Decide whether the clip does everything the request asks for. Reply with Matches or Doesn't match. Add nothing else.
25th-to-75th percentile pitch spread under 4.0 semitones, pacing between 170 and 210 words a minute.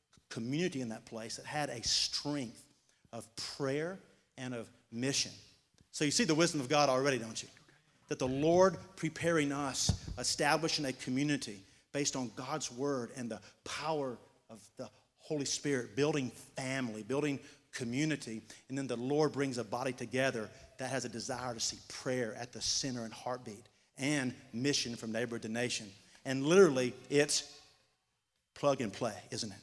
Doesn't match